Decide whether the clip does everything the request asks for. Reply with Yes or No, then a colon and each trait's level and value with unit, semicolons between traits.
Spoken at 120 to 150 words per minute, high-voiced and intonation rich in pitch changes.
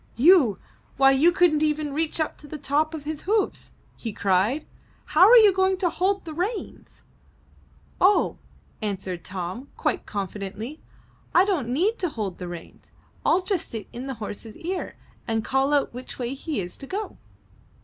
No: average, 170 wpm; very high, 290 Hz; wide, 8.0 semitones